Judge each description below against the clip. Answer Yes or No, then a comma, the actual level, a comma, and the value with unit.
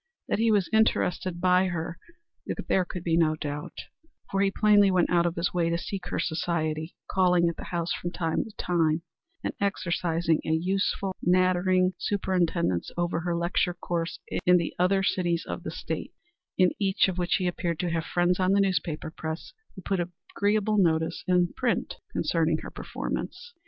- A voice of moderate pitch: Yes, medium, 175 Hz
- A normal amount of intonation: No, narrow, 2.0 semitones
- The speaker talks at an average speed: Yes, average, 175 wpm